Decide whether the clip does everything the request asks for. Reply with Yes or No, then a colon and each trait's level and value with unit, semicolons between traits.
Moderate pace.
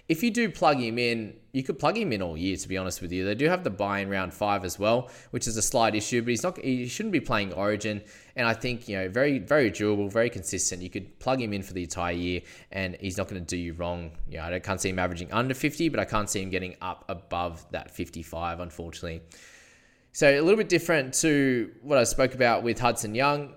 No: fast, 255 wpm